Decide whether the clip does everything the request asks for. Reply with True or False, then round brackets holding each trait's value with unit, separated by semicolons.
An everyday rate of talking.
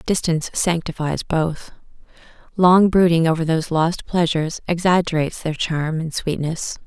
False (120 wpm)